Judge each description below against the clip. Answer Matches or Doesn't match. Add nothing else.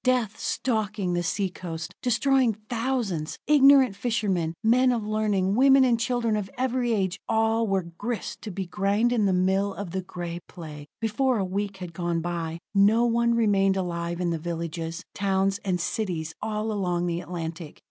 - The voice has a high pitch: Matches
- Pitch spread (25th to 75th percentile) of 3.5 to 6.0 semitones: Matches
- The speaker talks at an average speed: Matches